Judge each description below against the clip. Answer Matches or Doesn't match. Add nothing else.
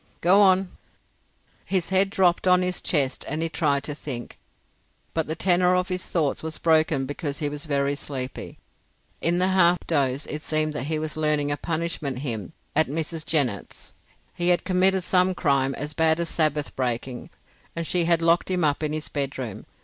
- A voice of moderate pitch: Matches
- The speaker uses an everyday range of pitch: Matches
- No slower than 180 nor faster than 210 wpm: Matches